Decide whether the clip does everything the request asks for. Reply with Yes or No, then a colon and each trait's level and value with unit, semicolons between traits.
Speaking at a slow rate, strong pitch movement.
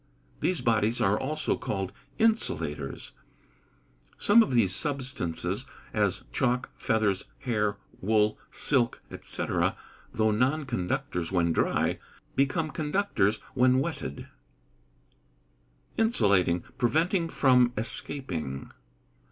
Yes: slow, 95 wpm; wide, 6.4 semitones